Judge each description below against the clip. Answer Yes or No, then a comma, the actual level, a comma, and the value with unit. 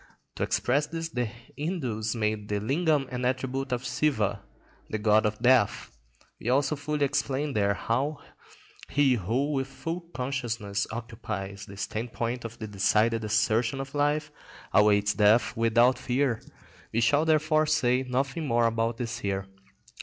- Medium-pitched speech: No, low, 120 Hz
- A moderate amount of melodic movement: Yes, average, 4.2 semitones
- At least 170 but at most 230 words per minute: No, average, 145 wpm